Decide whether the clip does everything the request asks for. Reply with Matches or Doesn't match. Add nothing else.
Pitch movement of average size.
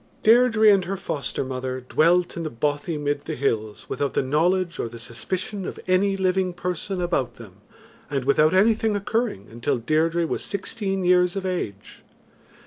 Doesn't match